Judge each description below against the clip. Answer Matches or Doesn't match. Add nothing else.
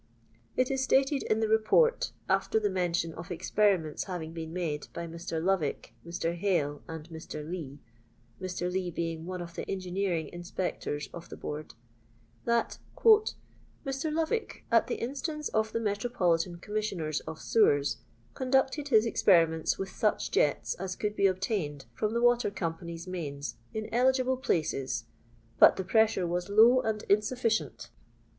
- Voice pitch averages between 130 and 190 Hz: Matches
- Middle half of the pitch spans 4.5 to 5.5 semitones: Matches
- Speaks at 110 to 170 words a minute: Matches